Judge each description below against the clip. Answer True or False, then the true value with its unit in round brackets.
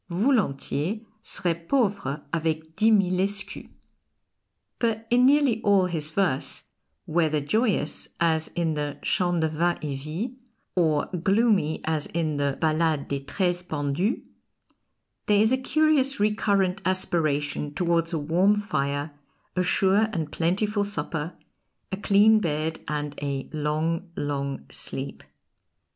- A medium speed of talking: False (125 wpm)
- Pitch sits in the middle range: True (170 Hz)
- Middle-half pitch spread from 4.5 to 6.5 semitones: True (5.0 semitones)